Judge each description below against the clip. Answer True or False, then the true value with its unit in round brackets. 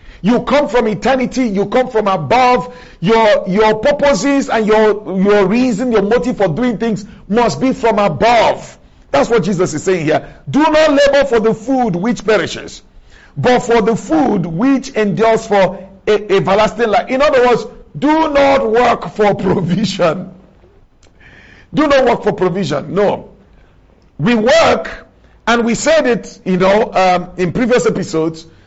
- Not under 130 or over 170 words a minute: True (155 wpm)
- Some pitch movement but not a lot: True (4.3 semitones)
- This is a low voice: False (225 Hz)